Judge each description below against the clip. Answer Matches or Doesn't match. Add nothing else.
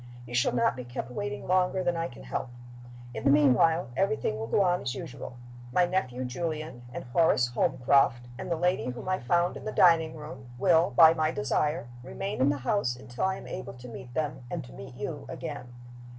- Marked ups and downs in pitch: Matches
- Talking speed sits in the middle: Doesn't match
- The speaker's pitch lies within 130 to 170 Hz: Matches